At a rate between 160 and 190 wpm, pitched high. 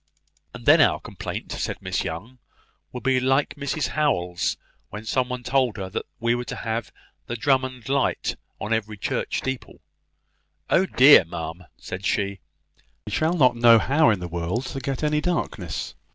No: average, 165 wpm; low, 125 Hz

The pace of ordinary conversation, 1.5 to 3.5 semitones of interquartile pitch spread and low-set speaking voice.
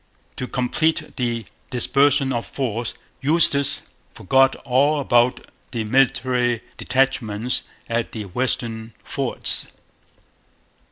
No: slow, 95 wpm; narrow, 2.5 semitones; low, 125 Hz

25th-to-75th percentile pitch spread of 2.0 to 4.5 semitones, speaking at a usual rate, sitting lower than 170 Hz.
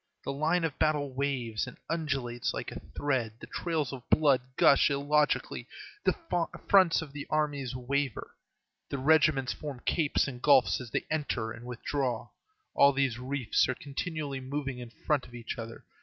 Yes: average, 3.1 semitones; average, 165 wpm; medium, 140 Hz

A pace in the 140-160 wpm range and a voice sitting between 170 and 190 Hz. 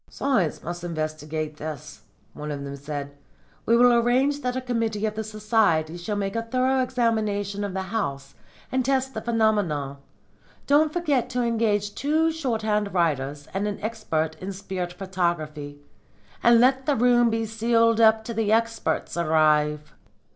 No: average, 155 wpm; high, 215 Hz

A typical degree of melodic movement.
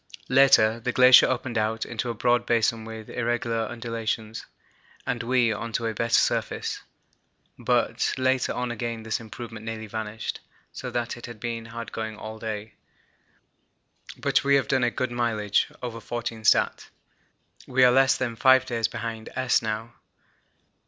No: narrow, 1.7 semitones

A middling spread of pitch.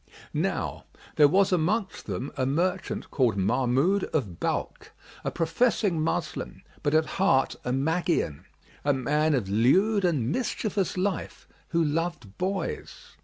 No: wide, 5.9 semitones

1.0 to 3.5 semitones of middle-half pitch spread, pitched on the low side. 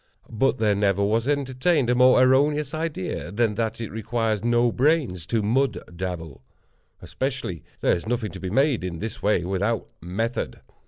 No: average, 4.7 semitones; low, 115 Hz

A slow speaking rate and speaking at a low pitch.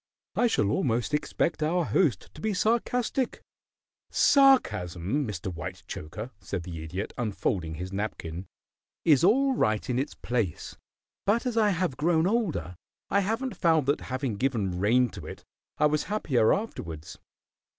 No: average, 145 wpm; low, 130 Hz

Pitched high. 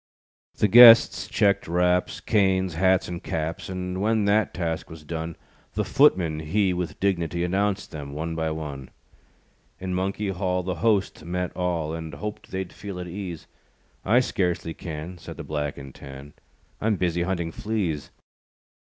No: very low, 90 Hz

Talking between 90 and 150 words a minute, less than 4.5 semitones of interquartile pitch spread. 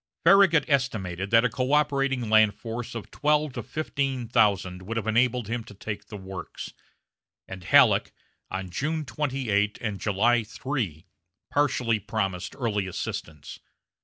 No: slow, 135 wpm; average, 4.9 semitones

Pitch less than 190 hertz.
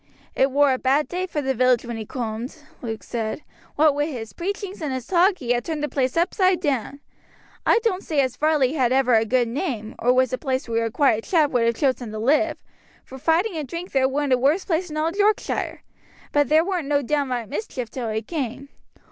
No: very high, 275 Hz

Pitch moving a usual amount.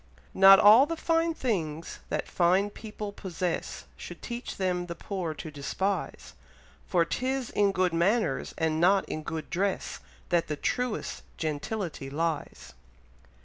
Yes: average, 4.3 semitones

